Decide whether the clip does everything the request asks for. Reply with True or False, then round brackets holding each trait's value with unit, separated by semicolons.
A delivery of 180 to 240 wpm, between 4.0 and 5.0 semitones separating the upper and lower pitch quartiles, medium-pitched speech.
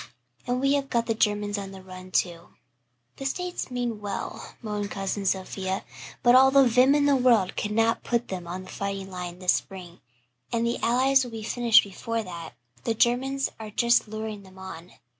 False (190 wpm; 4.4 semitones; 215 Hz)